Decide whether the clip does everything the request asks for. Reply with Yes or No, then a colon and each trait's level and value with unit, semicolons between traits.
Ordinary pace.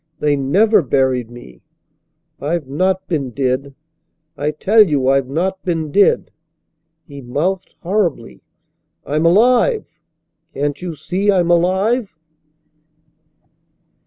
No: slow, 105 wpm